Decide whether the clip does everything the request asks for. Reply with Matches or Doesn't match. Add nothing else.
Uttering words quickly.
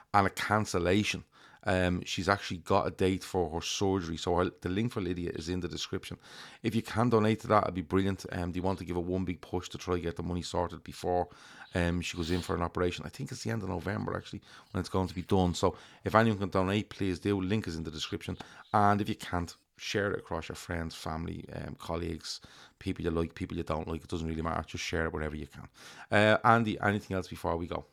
Matches